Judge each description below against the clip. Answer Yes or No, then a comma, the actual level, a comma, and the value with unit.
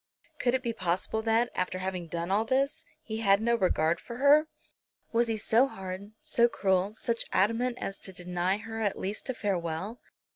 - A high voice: Yes, high, 215 Hz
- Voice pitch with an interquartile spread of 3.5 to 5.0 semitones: Yes, average, 4.0 semitones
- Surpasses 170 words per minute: Yes, average, 185 wpm